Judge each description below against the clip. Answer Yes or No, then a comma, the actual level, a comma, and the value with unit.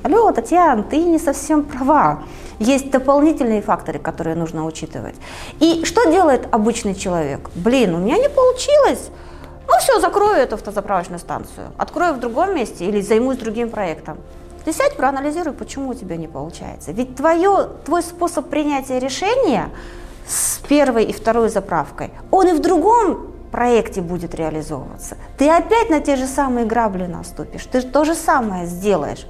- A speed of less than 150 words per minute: No, average, 155 wpm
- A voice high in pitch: Yes, very high, 260 Hz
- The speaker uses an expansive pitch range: Yes, wide, 8.0 semitones